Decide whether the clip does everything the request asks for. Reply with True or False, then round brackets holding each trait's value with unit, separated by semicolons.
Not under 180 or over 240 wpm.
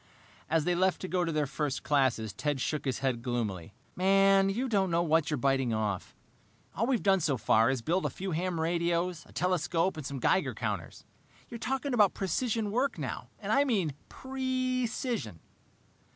True (185 wpm)